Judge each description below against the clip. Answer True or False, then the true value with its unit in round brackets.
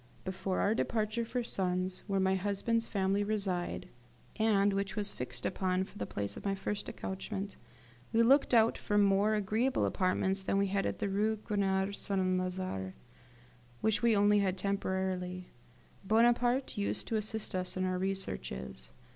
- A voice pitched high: True (195 Hz)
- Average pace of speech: True (160 wpm)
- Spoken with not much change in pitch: True (2.3 semitones)